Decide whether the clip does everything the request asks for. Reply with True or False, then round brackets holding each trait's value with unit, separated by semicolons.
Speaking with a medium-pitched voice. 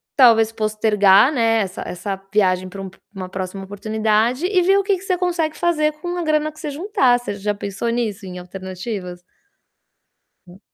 False (220 Hz)